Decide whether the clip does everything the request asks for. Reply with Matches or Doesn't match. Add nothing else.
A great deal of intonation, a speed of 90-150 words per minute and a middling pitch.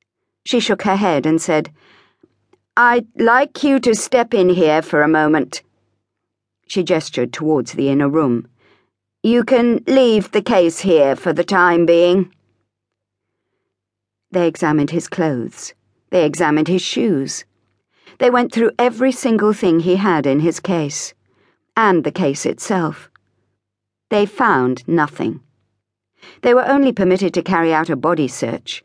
Matches